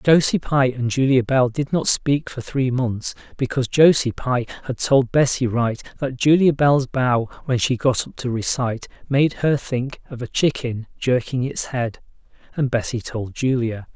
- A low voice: Yes, low, 130 Hz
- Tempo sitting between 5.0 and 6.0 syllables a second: No, 4.4 syllables/s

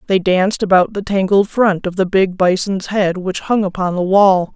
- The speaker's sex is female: Yes, female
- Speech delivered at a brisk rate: Yes, fast, 210 wpm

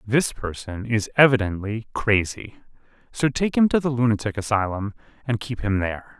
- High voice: No, low, 115 Hz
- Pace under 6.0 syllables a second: Yes, 5.1 syllables/s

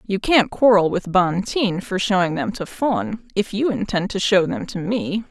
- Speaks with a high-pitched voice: Yes, high, 195 Hz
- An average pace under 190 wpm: No, fast, 205 wpm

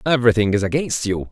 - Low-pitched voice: Yes, low, 115 Hz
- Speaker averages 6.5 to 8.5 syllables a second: Yes, 6.7 syllables/s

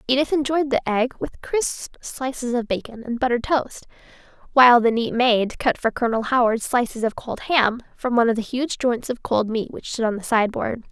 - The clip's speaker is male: No, female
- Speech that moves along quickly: Yes, fast, 210 wpm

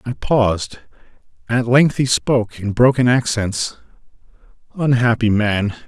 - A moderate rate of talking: No, slow, 110 wpm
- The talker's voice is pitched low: Yes, low, 115 Hz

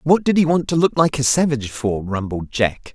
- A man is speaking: Yes, male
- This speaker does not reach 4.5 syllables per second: No, 5.4 syllables/s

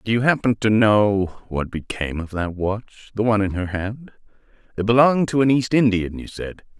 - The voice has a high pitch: No, low, 105 Hz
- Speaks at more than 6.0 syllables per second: No, 5.2 syllables/s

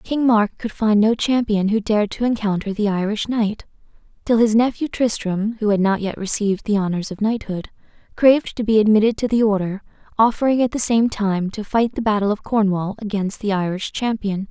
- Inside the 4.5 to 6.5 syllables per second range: Yes, 5.4 syllables/s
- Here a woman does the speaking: Yes, female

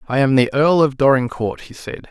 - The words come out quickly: Yes, fast, 230 wpm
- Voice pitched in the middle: No, low, 130 Hz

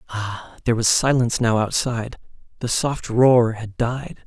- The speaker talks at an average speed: Yes, average, 155 wpm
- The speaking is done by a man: Yes, male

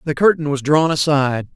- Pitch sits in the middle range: Yes, medium, 145 Hz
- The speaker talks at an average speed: Yes, average, 195 wpm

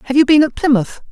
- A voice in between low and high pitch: No, very high, 280 Hz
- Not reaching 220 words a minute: No, fast, 270 wpm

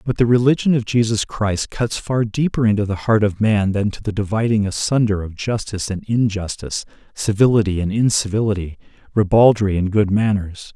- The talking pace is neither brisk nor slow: Yes, average, 165 wpm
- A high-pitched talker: No, low, 105 Hz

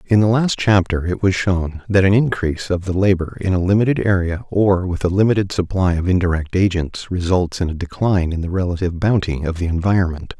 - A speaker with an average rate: No, fast, 210 wpm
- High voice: No, very low, 90 Hz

